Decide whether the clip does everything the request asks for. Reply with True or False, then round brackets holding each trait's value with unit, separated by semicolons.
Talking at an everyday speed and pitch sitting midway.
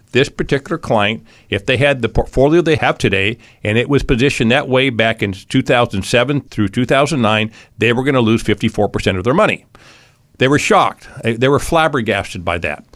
False (180 wpm; 120 Hz)